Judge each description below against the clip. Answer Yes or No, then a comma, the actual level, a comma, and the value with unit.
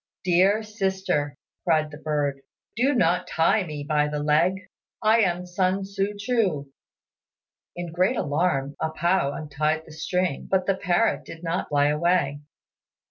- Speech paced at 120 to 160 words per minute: Yes, average, 145 wpm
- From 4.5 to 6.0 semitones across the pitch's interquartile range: No, average, 4.1 semitones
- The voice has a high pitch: No, medium, 175 Hz